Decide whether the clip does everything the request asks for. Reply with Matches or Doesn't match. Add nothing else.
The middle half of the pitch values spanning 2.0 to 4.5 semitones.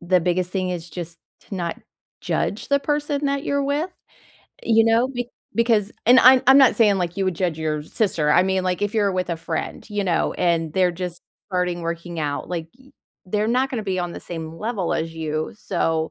Doesn't match